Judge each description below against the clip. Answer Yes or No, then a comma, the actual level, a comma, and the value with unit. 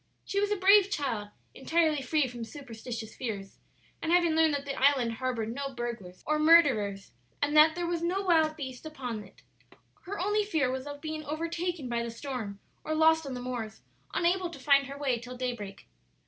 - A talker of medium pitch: No, very high, 280 Hz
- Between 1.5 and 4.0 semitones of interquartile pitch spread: No, average, 5.1 semitones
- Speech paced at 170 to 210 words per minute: Yes, average, 195 wpm